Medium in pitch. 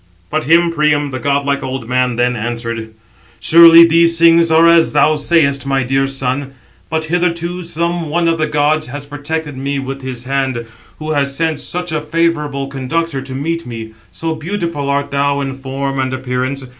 Yes: medium, 145 Hz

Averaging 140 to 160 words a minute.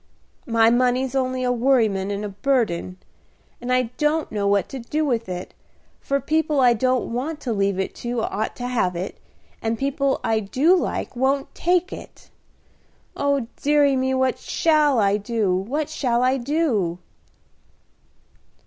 Yes: average, 155 wpm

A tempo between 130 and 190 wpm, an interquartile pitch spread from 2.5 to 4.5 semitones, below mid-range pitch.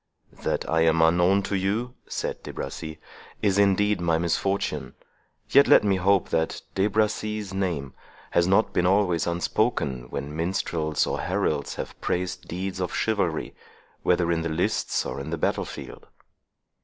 Yes: average, 155 wpm; average, 3.3 semitones; very low, 90 Hz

